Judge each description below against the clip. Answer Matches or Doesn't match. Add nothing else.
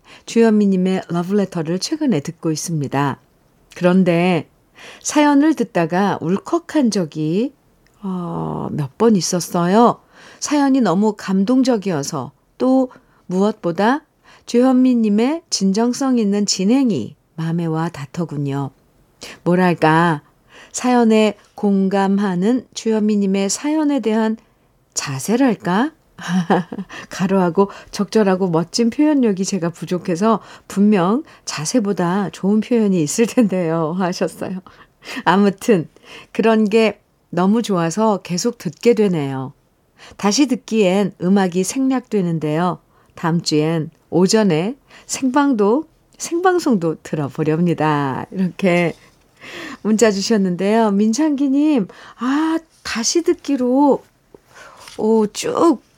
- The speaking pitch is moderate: Doesn't match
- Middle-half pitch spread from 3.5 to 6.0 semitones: Matches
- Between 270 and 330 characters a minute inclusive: Doesn't match